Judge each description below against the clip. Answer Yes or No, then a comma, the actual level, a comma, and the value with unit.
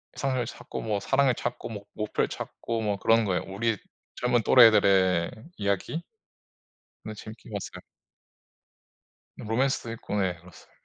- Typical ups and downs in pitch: Yes, average, 3.0 semitones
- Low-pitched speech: Yes, low, 110 Hz